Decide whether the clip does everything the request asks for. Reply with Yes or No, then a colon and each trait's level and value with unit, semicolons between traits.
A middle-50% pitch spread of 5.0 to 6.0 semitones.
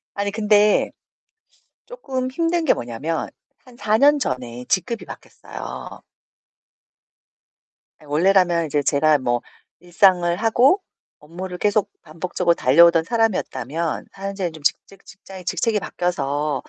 Yes: wide, 5.5 semitones